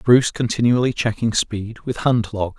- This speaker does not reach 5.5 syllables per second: Yes, 4.9 syllables/s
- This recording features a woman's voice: No, male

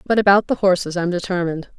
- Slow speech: No, average, 200 wpm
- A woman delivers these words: Yes, female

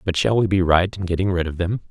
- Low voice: Yes, very low, 90 Hz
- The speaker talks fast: Yes, fast, 315 wpm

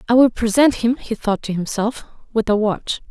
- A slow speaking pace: No, fast, 210 wpm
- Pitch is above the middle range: Yes, high, 225 Hz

